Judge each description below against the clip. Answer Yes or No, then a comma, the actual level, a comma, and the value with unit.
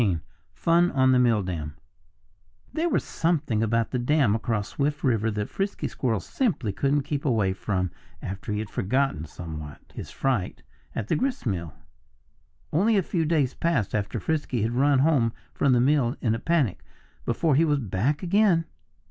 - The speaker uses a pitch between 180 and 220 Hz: No, low, 125 Hz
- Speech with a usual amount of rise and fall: No, wide, 6.4 semitones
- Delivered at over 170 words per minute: No, average, 165 wpm